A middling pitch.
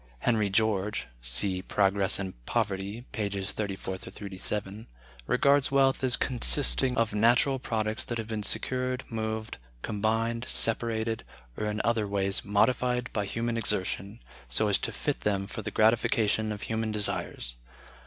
No: low, 110 Hz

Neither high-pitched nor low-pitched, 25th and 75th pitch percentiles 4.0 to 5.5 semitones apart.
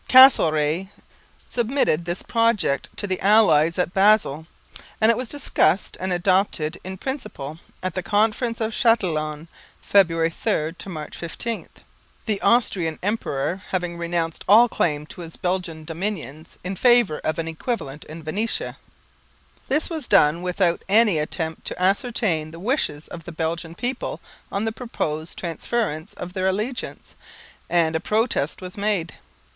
Yes: medium, 180 Hz; average, 5.2 semitones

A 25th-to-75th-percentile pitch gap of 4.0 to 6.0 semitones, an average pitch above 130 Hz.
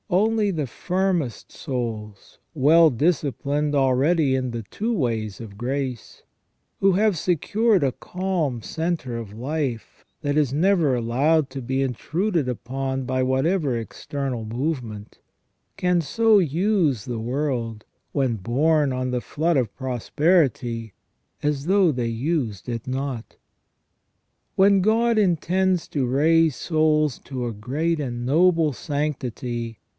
Yes: wide, 5.4 semitones; medium, 140 Hz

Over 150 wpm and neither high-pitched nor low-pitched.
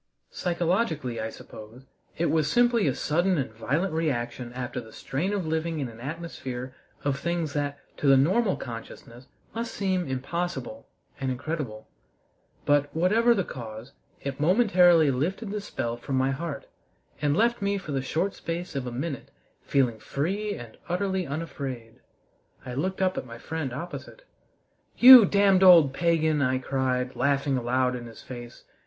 Yes: average, 160 wpm; medium, 145 Hz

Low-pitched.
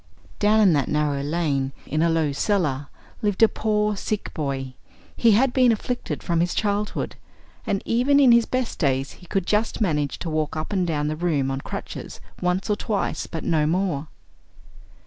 No: medium, 175 Hz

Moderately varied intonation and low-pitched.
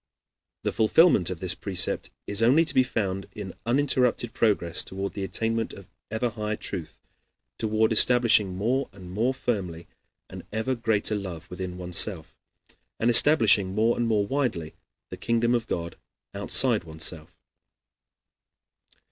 Yes: average, 4.2 semitones; low, 105 Hz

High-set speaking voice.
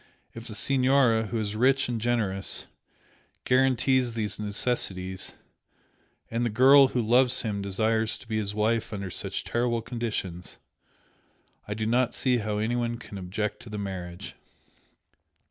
No: low, 115 Hz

